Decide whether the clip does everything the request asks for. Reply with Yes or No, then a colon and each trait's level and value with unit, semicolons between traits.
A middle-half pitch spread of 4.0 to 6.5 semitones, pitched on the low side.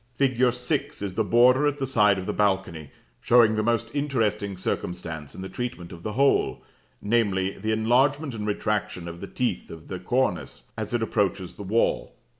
Yes: average, 4.5 semitones; low, 110 Hz